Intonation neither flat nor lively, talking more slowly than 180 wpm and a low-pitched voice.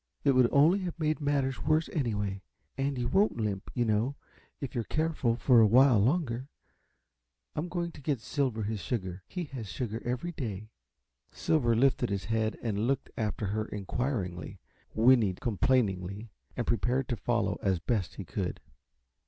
Yes: average, 4.6 semitones; average, 160 wpm; low, 120 Hz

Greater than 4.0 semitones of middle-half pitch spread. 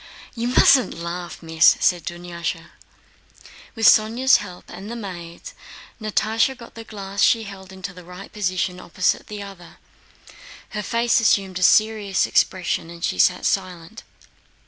No: average, 3.7 semitones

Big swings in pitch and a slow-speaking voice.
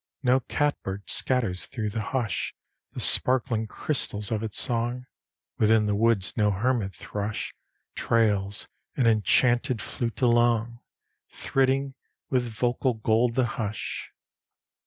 No: average, 2.9 semitones; slow, 115 wpm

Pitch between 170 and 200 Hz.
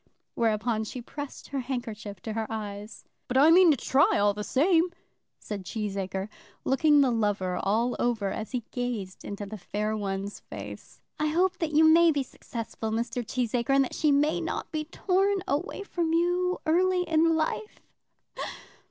No: very high, 250 Hz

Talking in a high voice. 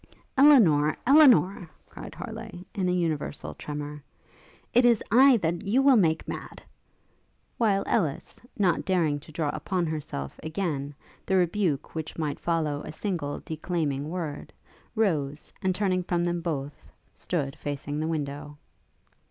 No: medium, 165 Hz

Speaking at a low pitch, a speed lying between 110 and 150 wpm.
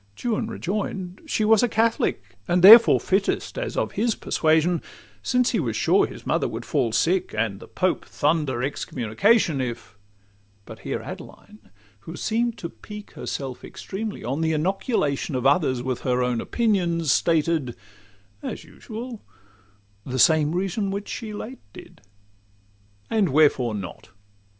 No: medium, 160 Hz; average, 140 wpm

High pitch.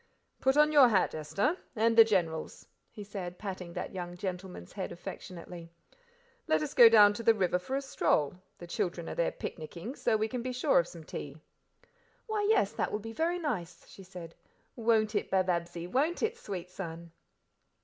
Yes: high, 195 Hz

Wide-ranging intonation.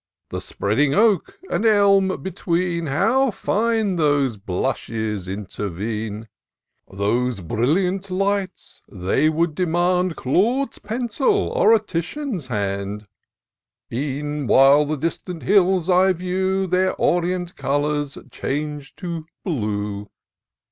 Yes: wide, 7.3 semitones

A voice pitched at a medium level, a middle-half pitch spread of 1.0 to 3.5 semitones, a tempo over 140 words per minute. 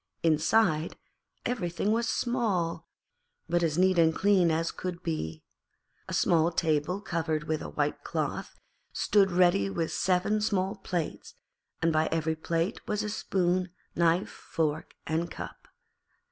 No: medium, 170 Hz; average, 2.9 semitones; slow, 135 wpm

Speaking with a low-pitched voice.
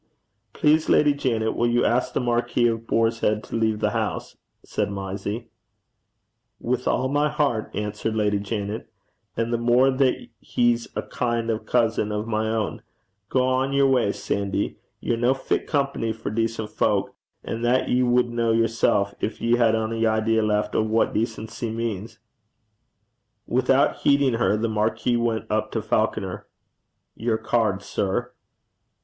Yes: low, 115 Hz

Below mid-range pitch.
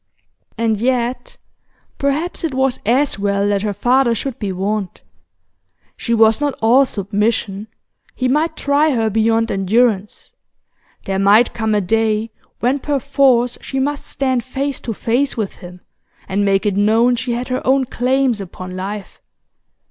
No: high, 230 Hz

